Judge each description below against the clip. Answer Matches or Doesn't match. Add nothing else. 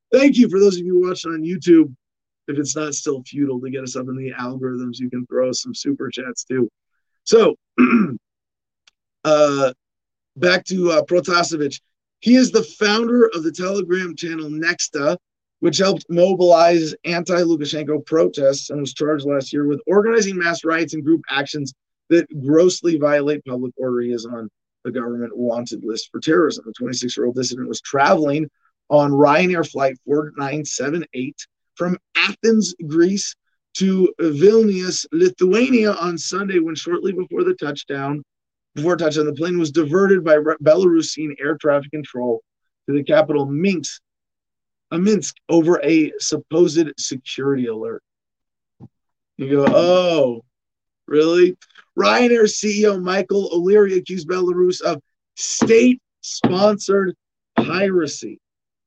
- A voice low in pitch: Doesn't match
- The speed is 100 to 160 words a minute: Matches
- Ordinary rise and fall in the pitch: Matches